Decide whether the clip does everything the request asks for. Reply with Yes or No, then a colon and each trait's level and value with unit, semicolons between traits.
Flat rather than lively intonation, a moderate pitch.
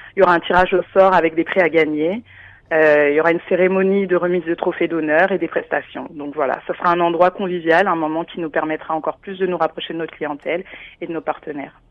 Yes: narrow, 2.2 semitones; medium, 170 Hz